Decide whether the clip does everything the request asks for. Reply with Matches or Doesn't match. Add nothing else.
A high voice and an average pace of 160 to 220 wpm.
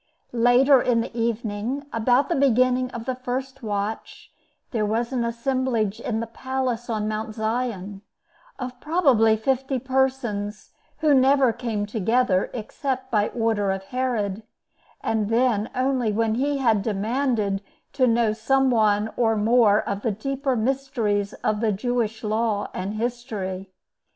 Doesn't match